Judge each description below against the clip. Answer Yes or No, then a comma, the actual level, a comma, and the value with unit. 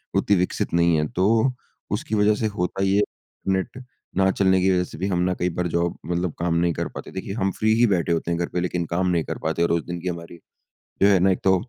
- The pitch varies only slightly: Yes, narrow, 2.2 semitones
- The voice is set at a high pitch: No, very low, 90 Hz